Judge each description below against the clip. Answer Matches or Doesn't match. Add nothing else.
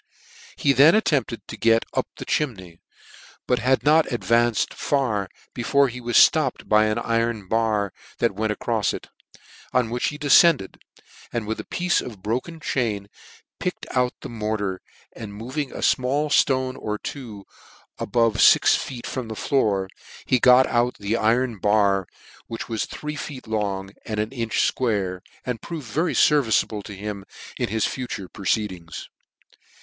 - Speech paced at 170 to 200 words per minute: Doesn't match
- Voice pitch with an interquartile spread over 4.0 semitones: Doesn't match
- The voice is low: Matches